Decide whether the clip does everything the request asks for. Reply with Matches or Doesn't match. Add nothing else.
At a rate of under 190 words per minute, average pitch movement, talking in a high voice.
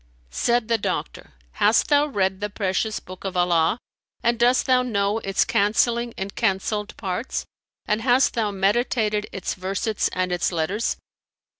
Matches